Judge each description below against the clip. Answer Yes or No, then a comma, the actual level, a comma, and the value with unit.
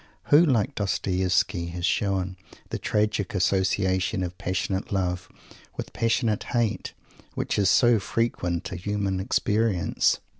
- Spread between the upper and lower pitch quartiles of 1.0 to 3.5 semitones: Yes, narrow, 2.6 semitones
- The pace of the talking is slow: Yes, slow, 120 wpm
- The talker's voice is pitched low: Yes, very low, 95 Hz